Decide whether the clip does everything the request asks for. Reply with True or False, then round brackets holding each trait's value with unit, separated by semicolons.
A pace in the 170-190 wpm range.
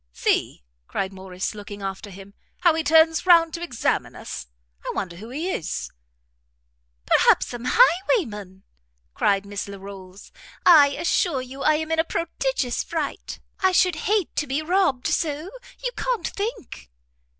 False (150 wpm)